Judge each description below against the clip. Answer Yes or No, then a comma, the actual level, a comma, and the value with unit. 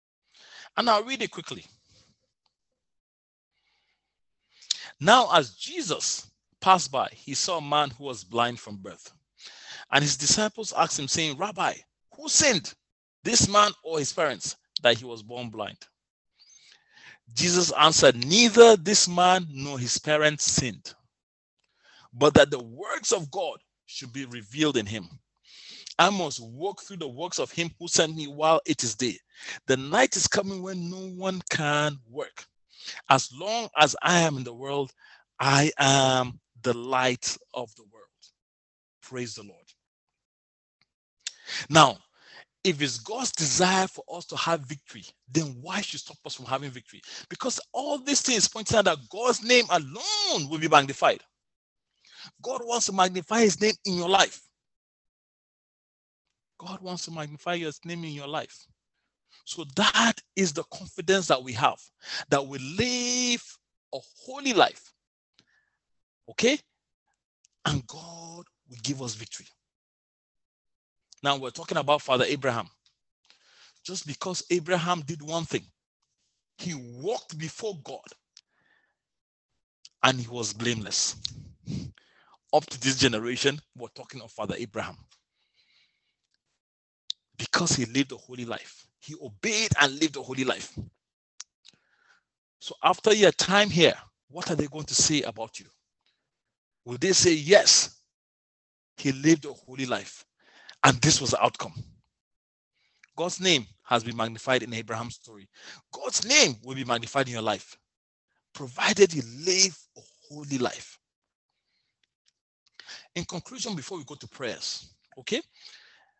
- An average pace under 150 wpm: Yes, average, 140 wpm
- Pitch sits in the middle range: Yes, medium, 150 Hz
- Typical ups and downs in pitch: No, wide, 6.5 semitones